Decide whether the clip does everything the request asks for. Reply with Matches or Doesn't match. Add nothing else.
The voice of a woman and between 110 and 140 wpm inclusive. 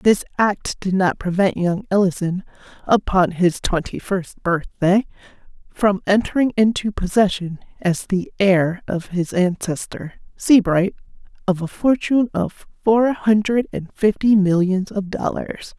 Matches